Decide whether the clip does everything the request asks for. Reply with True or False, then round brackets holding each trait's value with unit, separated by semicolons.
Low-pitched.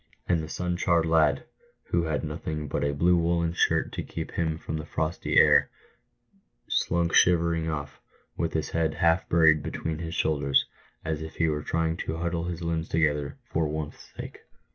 True (80 Hz)